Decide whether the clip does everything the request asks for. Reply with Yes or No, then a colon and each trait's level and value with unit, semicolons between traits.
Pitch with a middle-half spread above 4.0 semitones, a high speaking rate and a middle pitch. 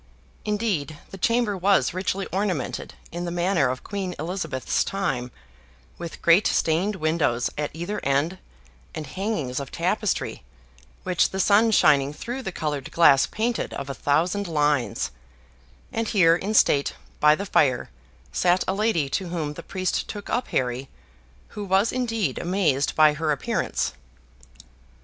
No: average, 5.2 semitones; average, 145 wpm; medium, 175 Hz